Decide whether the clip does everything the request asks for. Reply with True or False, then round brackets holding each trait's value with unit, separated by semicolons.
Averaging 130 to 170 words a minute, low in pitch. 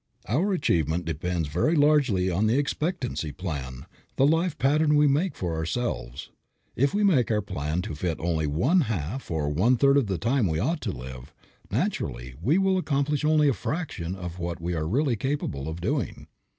False (185 wpm; 105 Hz)